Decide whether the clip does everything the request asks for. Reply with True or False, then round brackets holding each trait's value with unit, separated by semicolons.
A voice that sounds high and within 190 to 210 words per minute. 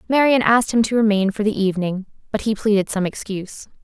True (210 Hz; 205 wpm)